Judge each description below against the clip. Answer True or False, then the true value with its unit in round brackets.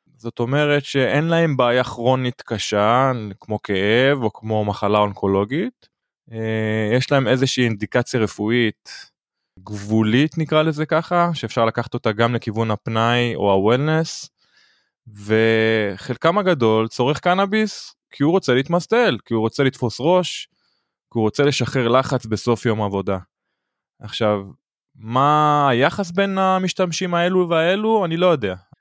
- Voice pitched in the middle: False (125 Hz)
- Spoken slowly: False (125 wpm)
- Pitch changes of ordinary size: False (6.0 semitones)